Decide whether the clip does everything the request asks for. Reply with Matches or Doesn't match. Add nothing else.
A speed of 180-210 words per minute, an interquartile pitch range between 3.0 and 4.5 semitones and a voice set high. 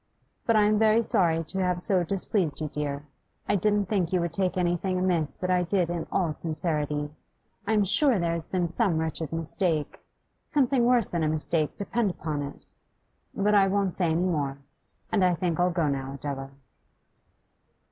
Doesn't match